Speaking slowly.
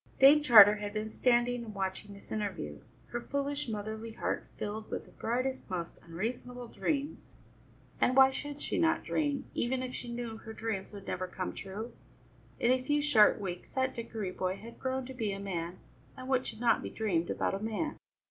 No: average, 195 wpm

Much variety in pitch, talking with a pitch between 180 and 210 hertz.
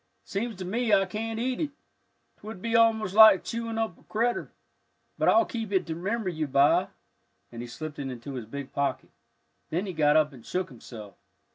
Yes: wide, 7.8 semitones; medium, 185 Hz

